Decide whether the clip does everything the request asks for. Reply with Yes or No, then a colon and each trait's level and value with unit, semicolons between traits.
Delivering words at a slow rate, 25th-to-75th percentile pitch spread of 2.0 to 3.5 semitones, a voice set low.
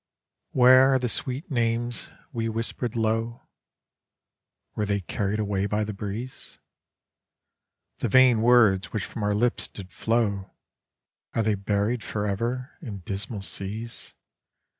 Yes: slow, 125 wpm; average, 2.9 semitones; low, 110 Hz